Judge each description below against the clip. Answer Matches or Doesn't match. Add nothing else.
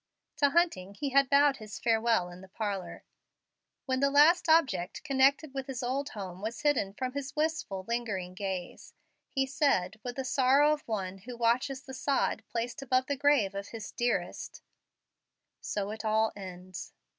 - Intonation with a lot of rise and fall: Matches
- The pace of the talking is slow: Doesn't match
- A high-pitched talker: Matches